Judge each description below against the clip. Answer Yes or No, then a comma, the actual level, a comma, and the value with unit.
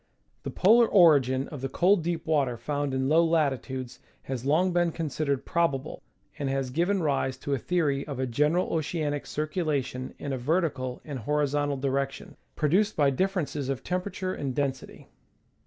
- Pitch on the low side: No, medium, 145 Hz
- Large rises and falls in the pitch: No, average, 3.8 semitones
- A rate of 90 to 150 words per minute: No, average, 160 wpm